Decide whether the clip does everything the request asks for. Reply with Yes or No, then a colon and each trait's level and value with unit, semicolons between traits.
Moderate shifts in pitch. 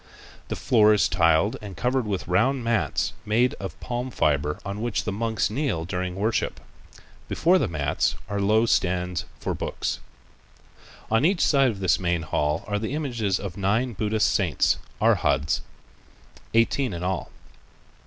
Yes: average, 4.6 semitones